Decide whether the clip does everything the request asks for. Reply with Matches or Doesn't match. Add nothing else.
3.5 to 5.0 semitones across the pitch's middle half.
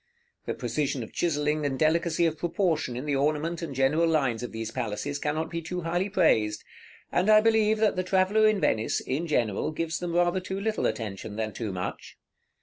Doesn't match